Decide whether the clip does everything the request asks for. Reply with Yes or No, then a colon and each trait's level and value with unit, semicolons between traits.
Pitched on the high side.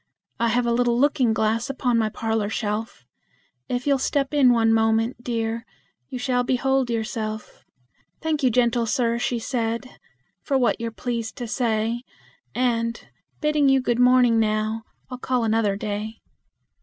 Yes: high, 235 Hz